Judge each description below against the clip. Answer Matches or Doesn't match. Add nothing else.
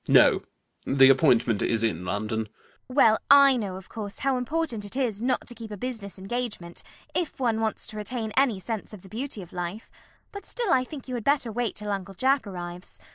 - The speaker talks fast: Matches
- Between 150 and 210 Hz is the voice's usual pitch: Doesn't match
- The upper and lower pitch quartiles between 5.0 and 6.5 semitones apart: Matches